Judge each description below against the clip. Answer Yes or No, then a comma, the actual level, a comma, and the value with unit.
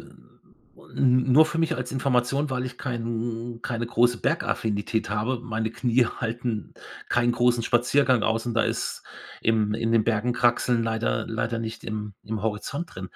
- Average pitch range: No, narrow, 1.8 semitones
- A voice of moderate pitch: No, low, 115 Hz